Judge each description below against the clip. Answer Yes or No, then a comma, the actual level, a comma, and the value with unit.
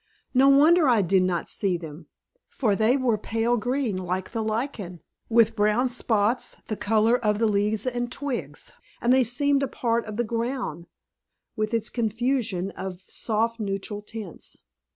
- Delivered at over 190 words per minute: No, average, 160 wpm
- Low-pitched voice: No, high, 225 Hz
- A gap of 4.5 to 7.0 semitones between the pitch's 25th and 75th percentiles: No, average, 3.3 semitones